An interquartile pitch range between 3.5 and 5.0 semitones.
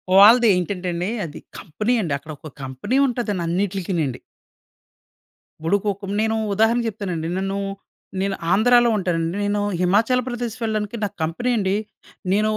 Yes: average, 3.8 semitones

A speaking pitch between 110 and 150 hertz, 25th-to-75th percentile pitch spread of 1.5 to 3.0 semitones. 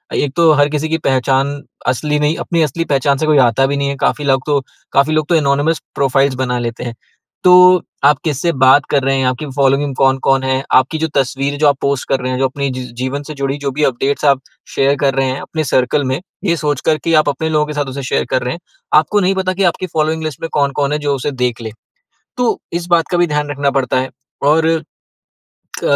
Yes: medium, 140 Hz; narrow, 2.5 semitones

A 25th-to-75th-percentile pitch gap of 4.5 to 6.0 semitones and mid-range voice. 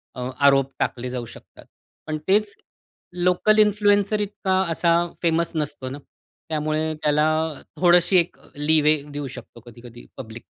Yes: average, 5.1 semitones; medium, 155 Hz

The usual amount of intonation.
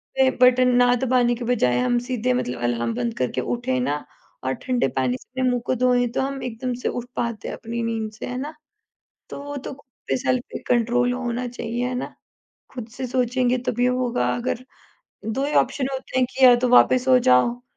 No: narrow, 1.5 semitones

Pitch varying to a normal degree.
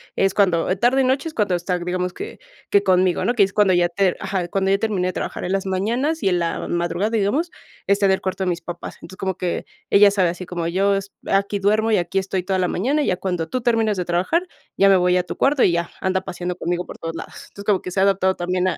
No: narrow, 2.2 semitones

